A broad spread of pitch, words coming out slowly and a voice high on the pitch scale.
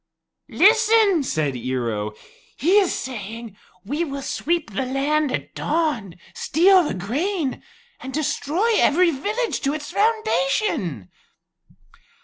Yes: wide, 8.4 semitones; slow, 120 wpm; very high, 290 Hz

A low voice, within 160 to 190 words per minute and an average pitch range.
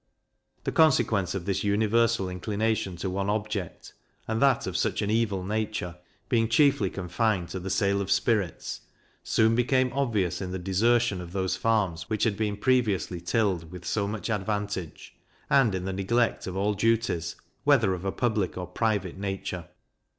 Yes: low, 100 Hz; average, 165 wpm; average, 3.3 semitones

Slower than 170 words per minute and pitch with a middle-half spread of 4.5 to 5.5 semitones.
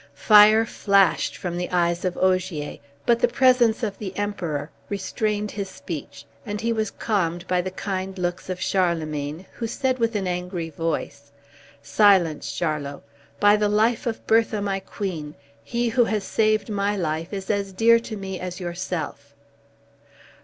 No: average, 160 wpm; average, 3.6 semitones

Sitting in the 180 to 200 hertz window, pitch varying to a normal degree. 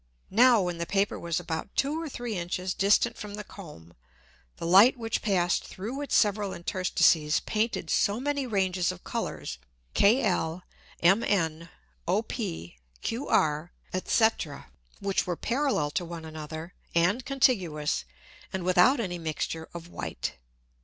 Yes: medium, 185 Hz; average, 5.0 semitones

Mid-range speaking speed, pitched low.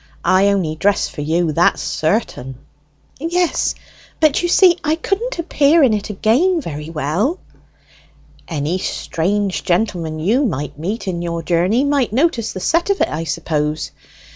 No: average, 150 wpm; high, 200 Hz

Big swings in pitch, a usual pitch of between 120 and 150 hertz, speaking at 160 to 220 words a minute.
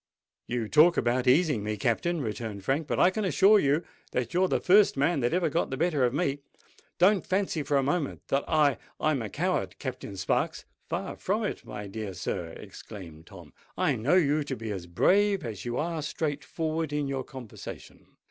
Yes: wide, 6.6 semitones; medium, 140 Hz; average, 195 wpm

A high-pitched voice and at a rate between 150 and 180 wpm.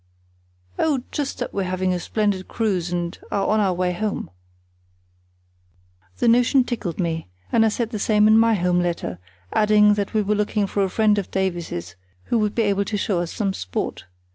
No: high, 200 Hz; average, 190 wpm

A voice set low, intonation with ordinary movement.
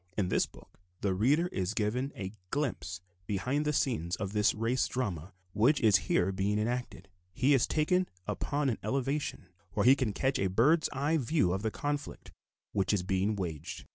No: low, 110 Hz; wide, 6.2 semitones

